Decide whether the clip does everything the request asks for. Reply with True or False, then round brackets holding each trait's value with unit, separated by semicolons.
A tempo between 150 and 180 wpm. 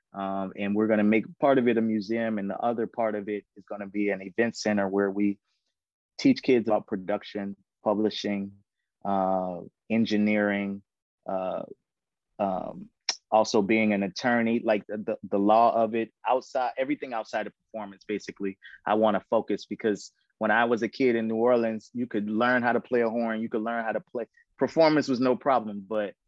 False (190 wpm)